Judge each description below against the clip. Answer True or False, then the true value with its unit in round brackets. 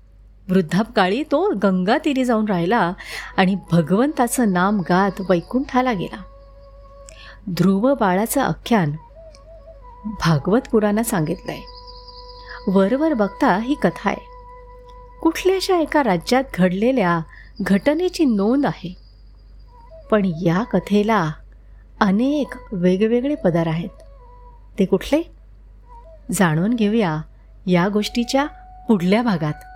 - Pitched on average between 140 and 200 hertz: False (210 Hz)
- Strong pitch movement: True (7.3 semitones)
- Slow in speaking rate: False (90 wpm)